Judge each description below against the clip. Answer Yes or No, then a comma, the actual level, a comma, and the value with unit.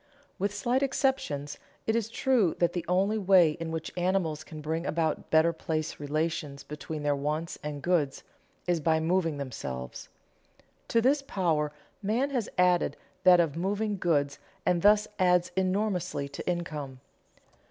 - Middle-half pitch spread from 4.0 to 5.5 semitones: Yes, average, 4.3 semitones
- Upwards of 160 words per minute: No, average, 150 wpm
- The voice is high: No, medium, 170 Hz